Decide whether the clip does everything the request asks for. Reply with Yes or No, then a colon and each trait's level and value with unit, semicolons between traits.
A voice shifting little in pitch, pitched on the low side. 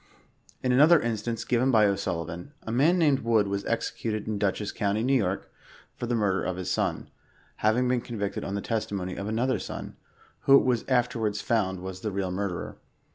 No: average, 3.7 semitones; low, 110 Hz